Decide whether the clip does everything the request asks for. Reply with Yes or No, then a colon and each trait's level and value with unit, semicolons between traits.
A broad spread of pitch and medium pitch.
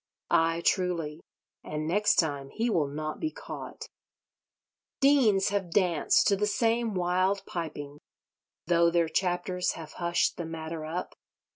No: average, 3.7 semitones; medium, 175 Hz